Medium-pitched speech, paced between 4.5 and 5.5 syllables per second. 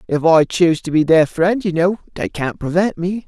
Yes: medium, 170 Hz; 5.1 syllables/s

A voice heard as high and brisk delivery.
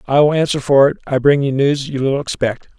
No: medium, 140 Hz; fast, 260 wpm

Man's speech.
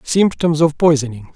Yes: male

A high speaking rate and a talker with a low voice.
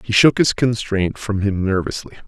No: average, 185 wpm; low, 105 Hz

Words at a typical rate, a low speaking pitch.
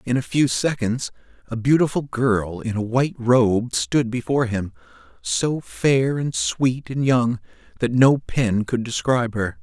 Yes: average, 160 wpm; low, 120 Hz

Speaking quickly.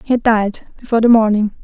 No: average, 185 wpm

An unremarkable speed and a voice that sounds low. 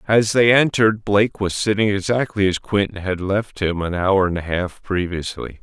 Yes: average, 190 wpm; low, 100 Hz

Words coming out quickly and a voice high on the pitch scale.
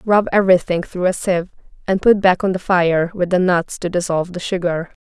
No: fast, 215 wpm; medium, 180 Hz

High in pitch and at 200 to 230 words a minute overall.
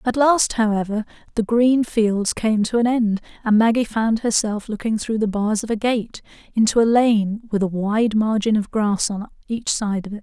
Yes: high, 220 Hz; fast, 205 wpm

